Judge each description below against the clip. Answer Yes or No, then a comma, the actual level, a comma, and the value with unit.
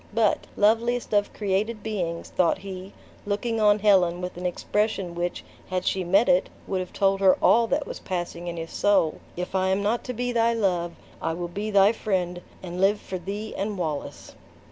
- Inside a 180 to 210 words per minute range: Yes, average, 195 wpm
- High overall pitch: Yes, high, 195 Hz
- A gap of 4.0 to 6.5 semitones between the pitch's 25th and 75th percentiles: No, average, 3.1 semitones